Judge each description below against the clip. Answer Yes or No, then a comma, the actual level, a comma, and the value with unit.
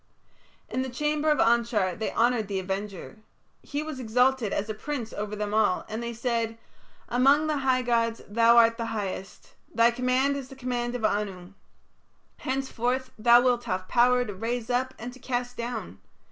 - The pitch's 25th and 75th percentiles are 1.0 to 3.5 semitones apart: Yes, average, 2.8 semitones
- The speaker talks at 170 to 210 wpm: Yes, average, 175 wpm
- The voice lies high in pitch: Yes, high, 235 Hz